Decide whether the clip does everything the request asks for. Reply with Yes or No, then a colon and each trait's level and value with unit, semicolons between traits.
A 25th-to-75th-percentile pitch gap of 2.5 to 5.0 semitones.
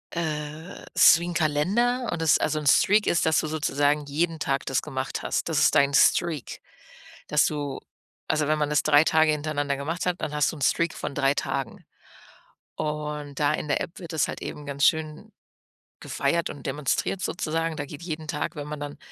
No: narrow, 2.0 semitones